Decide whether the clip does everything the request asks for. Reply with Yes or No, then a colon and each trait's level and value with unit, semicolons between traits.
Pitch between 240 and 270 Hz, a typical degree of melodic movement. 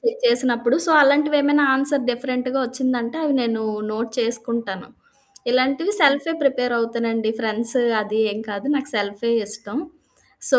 Yes: high, 245 Hz; average, 3.3 semitones